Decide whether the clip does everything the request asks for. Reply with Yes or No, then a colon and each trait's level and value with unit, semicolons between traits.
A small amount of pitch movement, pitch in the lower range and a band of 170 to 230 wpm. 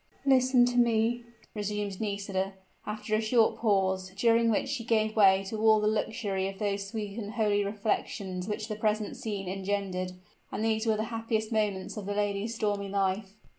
No: narrow, 2.0 semitones; high, 210 Hz; average, 175 wpm